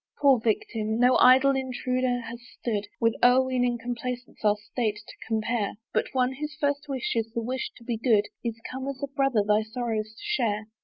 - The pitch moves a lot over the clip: No, average, 2.8 semitones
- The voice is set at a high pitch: Yes, high, 245 Hz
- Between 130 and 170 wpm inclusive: No, average, 190 wpm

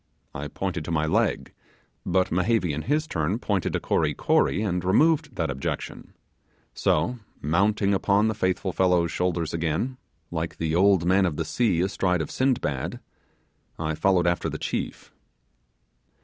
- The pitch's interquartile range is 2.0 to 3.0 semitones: No, average, 3.5 semitones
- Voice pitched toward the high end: No, very low, 90 Hz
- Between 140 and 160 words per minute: Yes, average, 150 wpm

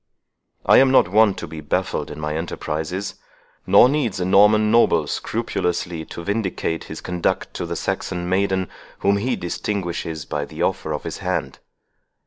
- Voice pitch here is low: Yes, very low, 90 Hz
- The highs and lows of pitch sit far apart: No, average, 4.1 semitones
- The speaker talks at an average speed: Yes, average, 160 wpm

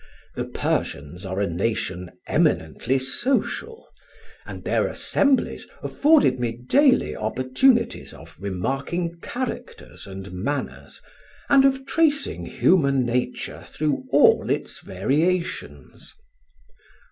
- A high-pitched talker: No, low, 135 Hz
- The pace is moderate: No, slow, 100 wpm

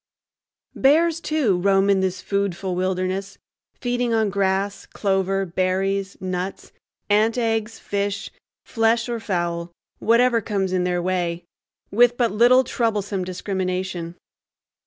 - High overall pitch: Yes, high, 195 Hz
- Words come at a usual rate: No, slow, 105 wpm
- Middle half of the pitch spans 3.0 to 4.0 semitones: Yes, average, 3.5 semitones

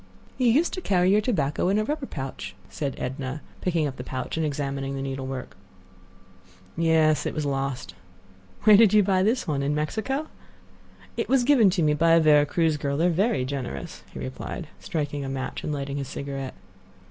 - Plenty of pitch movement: Yes, wide, 5.8 semitones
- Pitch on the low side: No, medium, 150 Hz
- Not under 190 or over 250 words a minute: Yes, average, 195 wpm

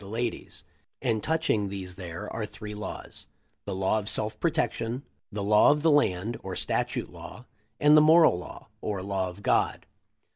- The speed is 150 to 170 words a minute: No, average, 180 wpm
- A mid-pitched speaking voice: No, low, 105 Hz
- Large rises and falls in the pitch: No, average, 4.2 semitones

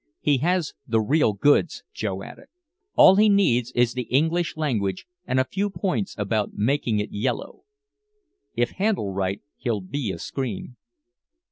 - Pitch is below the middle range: Yes, low, 125 Hz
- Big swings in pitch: Yes, wide, 7.6 semitones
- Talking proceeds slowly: No, average, 150 wpm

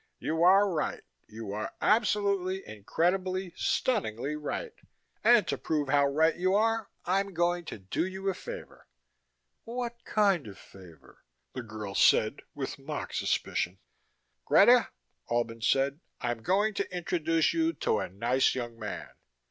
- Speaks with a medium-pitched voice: Yes, medium, 165 Hz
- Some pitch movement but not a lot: No, wide, 8.6 semitones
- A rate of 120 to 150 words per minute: Yes, average, 140 wpm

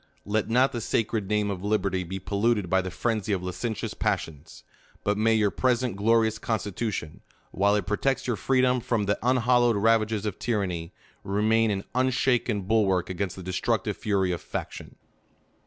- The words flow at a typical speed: Yes, average, 170 wpm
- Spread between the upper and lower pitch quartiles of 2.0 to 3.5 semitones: Yes, average, 3.1 semitones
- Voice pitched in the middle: No, low, 105 Hz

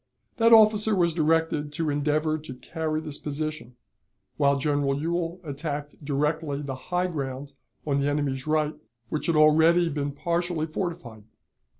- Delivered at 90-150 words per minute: Yes, average, 140 wpm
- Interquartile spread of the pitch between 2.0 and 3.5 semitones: Yes, narrow, 2.5 semitones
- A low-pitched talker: No, medium, 155 Hz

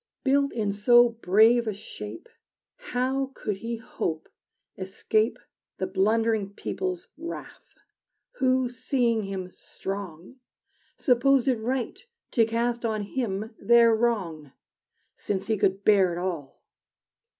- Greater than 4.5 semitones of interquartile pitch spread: No, average, 4.0 semitones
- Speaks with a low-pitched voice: No, high, 225 Hz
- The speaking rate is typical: No, slow, 115 wpm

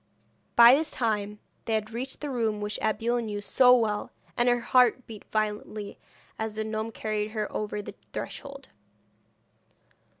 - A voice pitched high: Yes, high, 220 Hz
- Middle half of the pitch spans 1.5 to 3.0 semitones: Yes, narrow, 2.4 semitones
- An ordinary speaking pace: Yes, average, 155 wpm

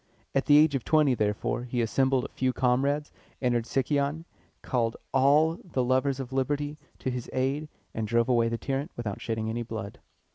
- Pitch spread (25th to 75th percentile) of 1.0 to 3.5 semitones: Yes, average, 3.1 semitones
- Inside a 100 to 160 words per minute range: No, average, 180 wpm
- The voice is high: No, low, 130 Hz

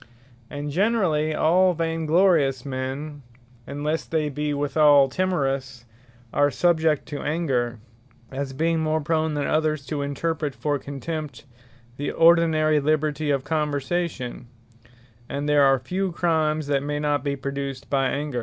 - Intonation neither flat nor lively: No, narrow, 2.3 semitones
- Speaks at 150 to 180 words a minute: No, slow, 135 wpm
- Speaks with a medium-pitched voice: Yes, medium, 150 Hz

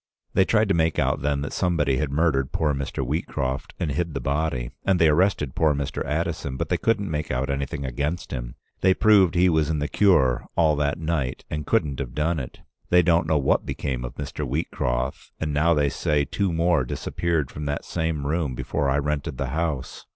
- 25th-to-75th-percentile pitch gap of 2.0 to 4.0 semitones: Yes, average, 3.3 semitones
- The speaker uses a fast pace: Yes, fast, 210 wpm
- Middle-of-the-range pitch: No, very low, 75 Hz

